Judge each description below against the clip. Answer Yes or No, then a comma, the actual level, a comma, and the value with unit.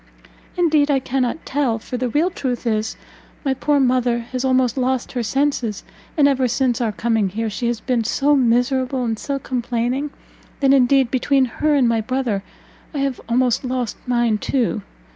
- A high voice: Yes, very high, 255 Hz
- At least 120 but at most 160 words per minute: No, average, 175 wpm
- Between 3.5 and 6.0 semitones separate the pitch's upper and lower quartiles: No, narrow, 2.4 semitones